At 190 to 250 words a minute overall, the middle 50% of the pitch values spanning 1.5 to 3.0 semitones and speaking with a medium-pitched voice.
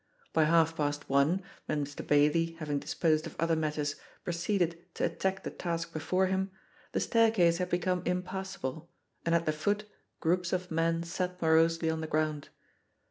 No: average, 165 wpm; narrow, 2.6 semitones; medium, 165 Hz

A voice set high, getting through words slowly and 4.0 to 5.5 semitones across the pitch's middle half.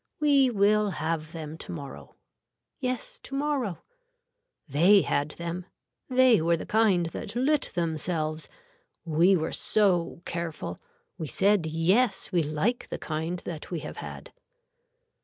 No: medium, 175 Hz; slow, 130 wpm; average, 5.1 semitones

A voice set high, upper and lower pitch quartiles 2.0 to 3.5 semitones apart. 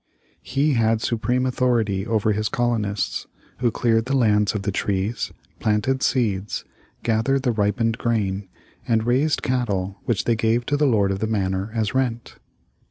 No: low, 115 Hz; average, 2.9 semitones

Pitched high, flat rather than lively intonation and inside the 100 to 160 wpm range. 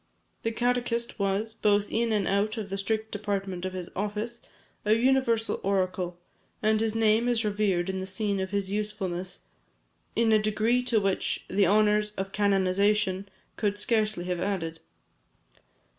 Yes: high, 210 Hz; narrow, 2.3 semitones; average, 155 wpm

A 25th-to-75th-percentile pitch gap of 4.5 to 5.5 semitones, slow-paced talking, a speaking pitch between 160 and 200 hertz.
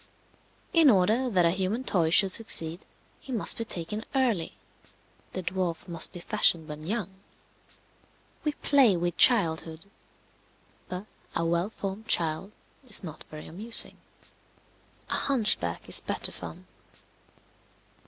Yes: average, 5.1 semitones; slow, 125 wpm; high, 190 Hz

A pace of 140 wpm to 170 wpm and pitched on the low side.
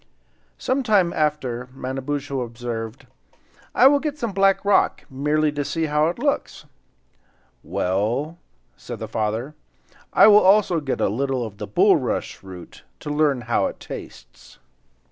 No: average, 150 wpm; medium, 145 Hz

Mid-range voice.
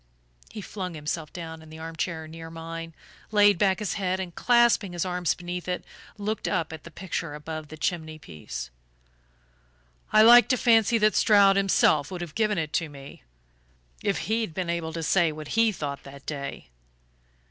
Yes: medium, 170 Hz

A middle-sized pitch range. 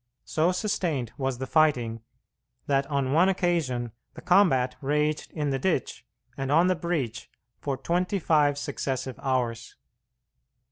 Yes: average, 4.5 semitones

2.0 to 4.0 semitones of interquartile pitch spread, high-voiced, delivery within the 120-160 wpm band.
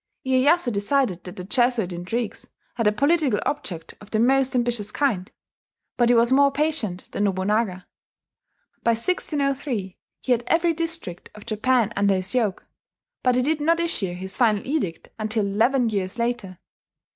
No: average, 5.2 semitones; high, 235 Hz; average, 155 wpm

